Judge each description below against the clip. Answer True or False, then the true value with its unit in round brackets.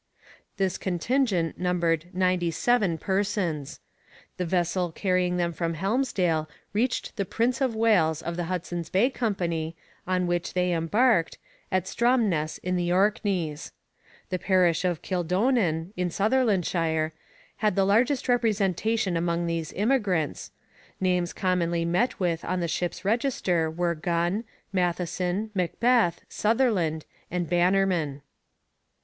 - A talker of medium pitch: True (180 Hz)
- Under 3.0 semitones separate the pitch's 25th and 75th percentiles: False (3.4 semitones)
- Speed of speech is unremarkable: False (120 wpm)